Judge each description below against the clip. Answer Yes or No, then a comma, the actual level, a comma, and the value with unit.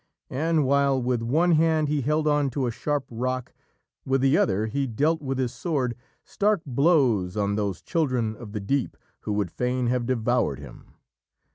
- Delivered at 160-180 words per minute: Yes, average, 175 wpm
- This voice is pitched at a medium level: No, low, 130 Hz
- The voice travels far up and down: No, average, 4.1 semitones